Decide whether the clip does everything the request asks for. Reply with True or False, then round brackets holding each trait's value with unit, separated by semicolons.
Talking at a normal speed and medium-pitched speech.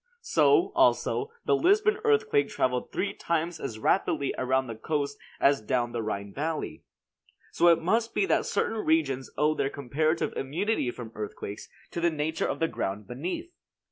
True (165 wpm; 155 Hz)